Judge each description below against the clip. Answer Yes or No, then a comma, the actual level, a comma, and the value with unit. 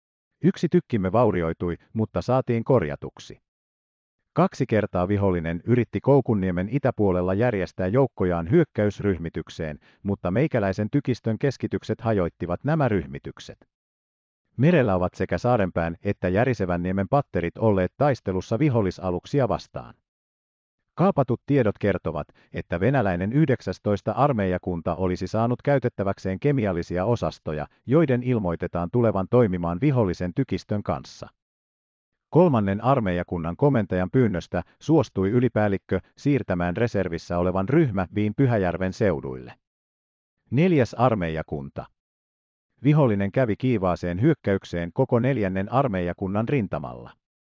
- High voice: No, low, 100 Hz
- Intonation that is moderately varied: No, wide, 6.1 semitones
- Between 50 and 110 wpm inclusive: Yes, slow, 95 wpm